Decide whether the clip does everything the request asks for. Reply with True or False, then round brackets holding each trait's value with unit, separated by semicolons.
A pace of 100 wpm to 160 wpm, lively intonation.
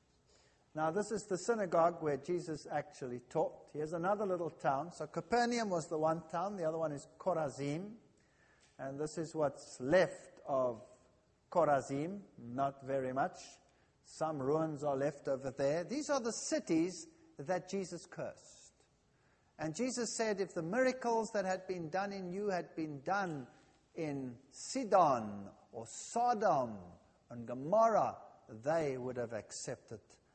True (140 wpm; 5.9 semitones)